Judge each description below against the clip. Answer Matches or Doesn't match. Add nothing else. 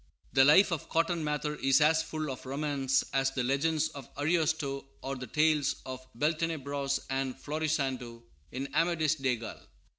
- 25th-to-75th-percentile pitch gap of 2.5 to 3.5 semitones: Matches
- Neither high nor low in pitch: Matches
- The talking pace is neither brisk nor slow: Matches